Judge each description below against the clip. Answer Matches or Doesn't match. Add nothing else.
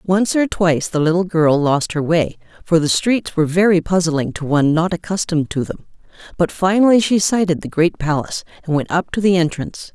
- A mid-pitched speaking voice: Matches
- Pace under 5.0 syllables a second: Doesn't match